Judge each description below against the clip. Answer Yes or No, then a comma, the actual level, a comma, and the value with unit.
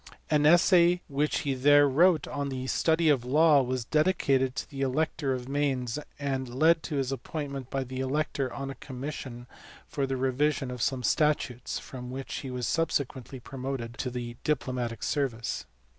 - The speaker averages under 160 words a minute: No, average, 175 wpm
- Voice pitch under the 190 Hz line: Yes, low, 135 Hz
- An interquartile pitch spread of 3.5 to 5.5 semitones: No, average, 2.7 semitones